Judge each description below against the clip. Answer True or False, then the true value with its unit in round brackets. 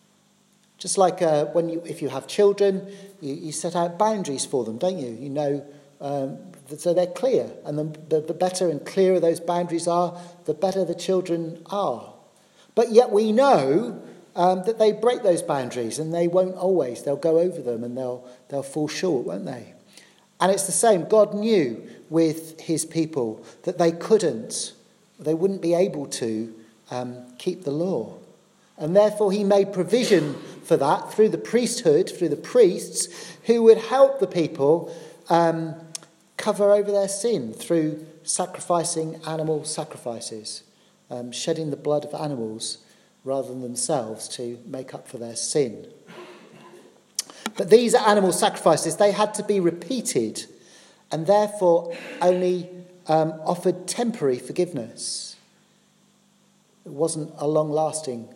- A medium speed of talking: True (150 wpm)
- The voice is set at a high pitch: False (170 Hz)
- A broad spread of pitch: False (4.8 semitones)